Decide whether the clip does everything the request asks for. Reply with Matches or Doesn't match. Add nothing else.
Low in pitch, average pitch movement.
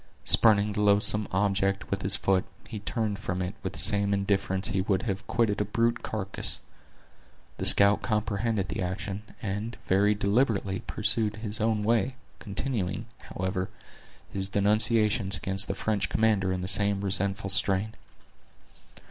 Doesn't match